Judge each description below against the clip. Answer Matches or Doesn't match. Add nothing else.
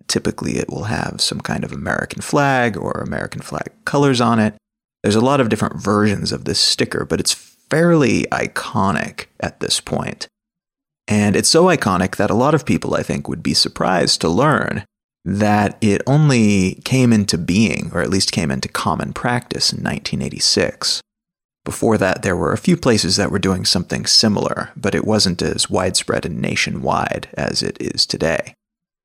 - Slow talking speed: Doesn't match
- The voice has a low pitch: Matches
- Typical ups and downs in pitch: Doesn't match